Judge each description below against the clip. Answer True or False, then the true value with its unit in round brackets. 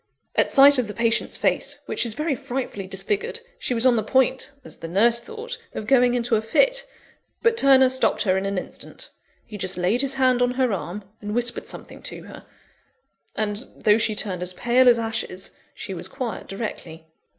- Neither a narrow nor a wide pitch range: True (4.4 semitones)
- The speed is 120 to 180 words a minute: False (195 wpm)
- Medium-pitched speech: False (235 Hz)